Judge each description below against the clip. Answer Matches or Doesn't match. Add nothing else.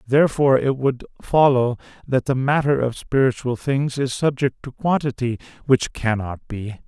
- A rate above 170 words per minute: Doesn't match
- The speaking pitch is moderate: Doesn't match